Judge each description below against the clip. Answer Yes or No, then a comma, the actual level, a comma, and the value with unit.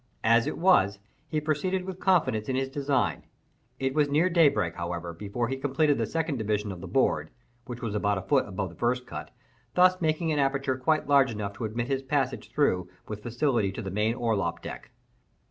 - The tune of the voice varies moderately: No, wide, 5.9 semitones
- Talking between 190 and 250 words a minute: Yes, average, 200 wpm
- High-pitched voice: No, low, 130 Hz